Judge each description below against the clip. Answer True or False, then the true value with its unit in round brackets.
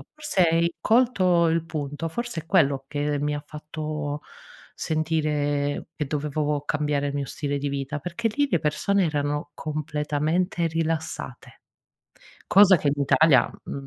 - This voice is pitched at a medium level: True (150 Hz)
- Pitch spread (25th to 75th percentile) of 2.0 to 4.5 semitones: True (2.4 semitones)